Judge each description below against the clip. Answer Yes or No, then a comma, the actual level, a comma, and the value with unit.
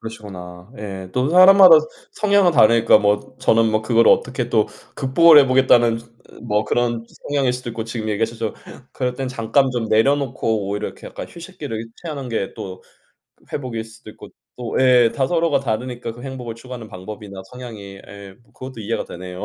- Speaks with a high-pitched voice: No, low, 115 Hz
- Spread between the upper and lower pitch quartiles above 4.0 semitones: No, average, 3.4 semitones